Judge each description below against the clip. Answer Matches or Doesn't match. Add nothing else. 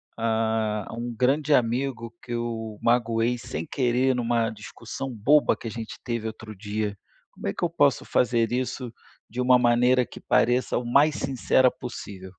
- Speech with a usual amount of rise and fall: Doesn't match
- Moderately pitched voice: Doesn't match